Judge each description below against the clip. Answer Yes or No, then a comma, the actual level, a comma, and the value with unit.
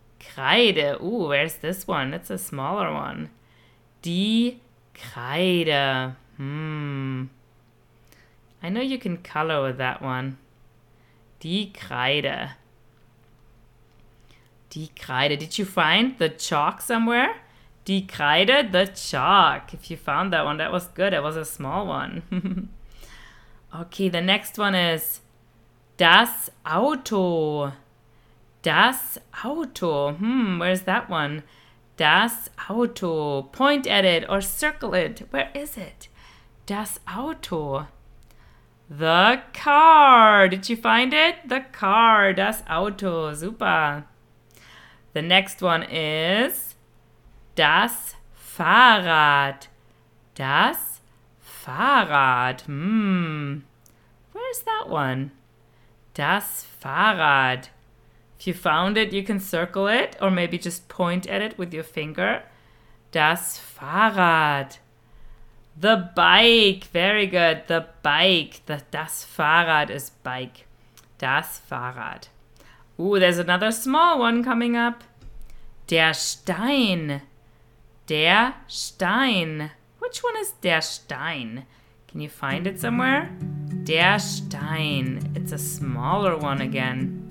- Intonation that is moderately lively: No, wide, 7.3 semitones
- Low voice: No, medium, 160 Hz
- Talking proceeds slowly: Yes, slow, 110 wpm